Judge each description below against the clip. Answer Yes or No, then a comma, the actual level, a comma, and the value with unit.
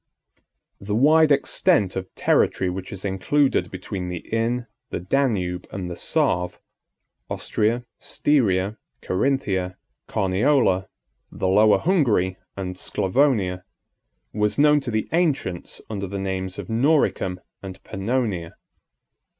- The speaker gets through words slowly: Yes, slow, 110 wpm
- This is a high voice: No, low, 100 Hz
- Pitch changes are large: Yes, wide, 6.0 semitones